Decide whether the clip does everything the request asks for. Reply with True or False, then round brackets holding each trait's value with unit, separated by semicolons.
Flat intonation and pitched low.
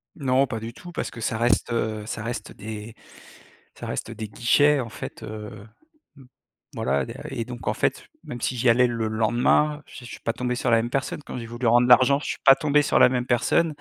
True (2.3 semitones; 120 Hz)